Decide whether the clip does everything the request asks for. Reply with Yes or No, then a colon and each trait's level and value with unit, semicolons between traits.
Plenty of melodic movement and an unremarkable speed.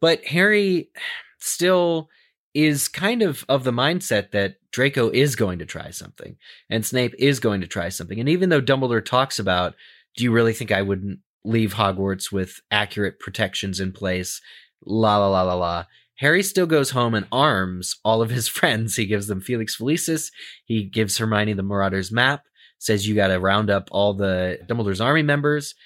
Yes: wide, 6.3 semitones; average, 185 wpm